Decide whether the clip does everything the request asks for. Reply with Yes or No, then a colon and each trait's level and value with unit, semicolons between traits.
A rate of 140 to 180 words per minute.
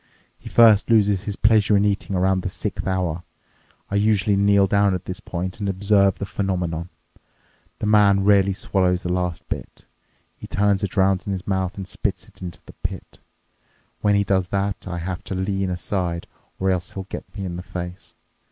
No: average, 190 wpm